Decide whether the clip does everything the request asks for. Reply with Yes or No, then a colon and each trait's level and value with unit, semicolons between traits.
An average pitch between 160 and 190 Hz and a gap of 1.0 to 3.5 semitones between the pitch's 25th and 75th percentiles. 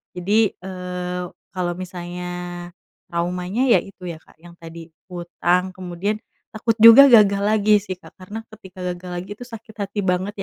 Yes: medium, 185 Hz; narrow, 2.5 semitones